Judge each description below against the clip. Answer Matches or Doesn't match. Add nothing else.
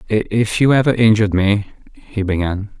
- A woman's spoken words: Doesn't match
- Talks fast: Doesn't match